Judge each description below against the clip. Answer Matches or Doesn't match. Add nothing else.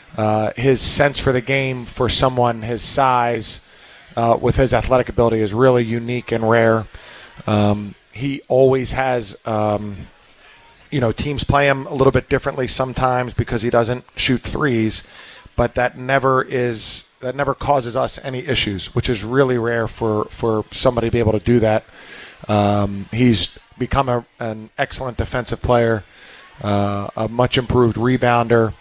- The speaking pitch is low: Matches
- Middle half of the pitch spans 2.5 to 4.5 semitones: Matches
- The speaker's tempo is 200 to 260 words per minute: Doesn't match